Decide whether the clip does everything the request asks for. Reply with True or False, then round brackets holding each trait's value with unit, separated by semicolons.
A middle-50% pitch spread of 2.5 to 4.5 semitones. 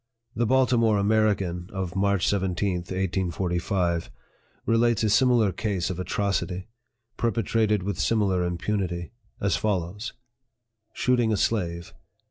True (3.5 semitones)